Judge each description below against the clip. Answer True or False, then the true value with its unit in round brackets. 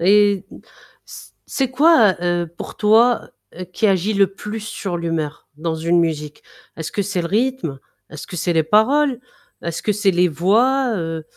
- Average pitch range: True (4.5 semitones)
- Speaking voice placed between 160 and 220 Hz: True (190 Hz)